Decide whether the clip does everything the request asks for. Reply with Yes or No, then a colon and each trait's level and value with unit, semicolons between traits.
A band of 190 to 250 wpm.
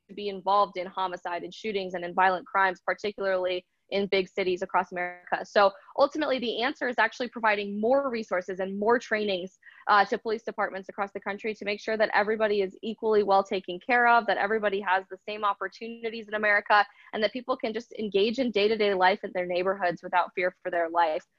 Yes: average, 200 wpm